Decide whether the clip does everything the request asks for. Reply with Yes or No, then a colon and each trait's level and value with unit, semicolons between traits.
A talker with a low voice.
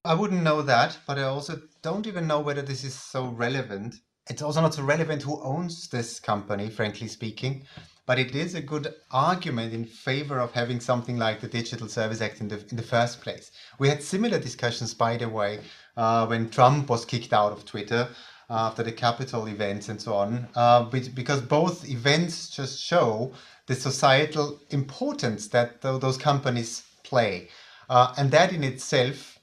Yes: low, 125 Hz